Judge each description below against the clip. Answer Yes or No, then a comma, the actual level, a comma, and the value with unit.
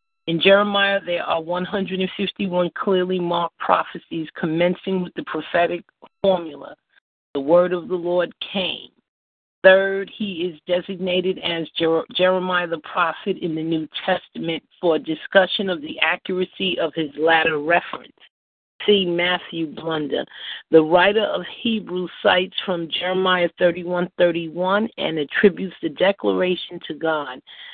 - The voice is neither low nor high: Yes, medium, 180 Hz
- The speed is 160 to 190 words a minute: No, average, 140 wpm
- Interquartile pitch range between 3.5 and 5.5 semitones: No, narrow, 2.4 semitones